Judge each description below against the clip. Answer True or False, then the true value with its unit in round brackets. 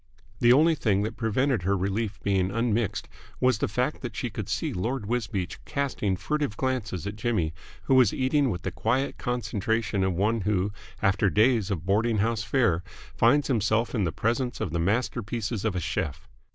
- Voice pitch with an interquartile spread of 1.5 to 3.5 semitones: False (3.9 semitones)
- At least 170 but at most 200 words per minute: True (180 wpm)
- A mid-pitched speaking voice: False (110 Hz)